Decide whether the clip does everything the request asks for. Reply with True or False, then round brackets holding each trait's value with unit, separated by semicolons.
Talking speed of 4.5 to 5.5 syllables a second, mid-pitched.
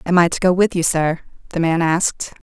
False (5.8 syllables/s; 170 Hz)